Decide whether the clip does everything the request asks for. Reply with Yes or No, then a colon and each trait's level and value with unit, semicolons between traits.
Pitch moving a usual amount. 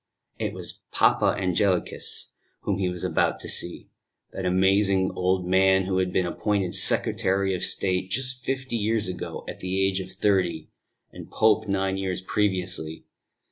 No: narrow, 1.4 semitones